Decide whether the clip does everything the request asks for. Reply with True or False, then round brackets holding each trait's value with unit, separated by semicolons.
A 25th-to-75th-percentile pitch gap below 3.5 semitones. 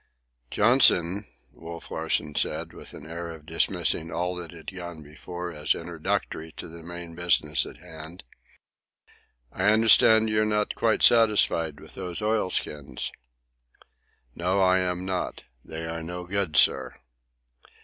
True (2.7 semitones)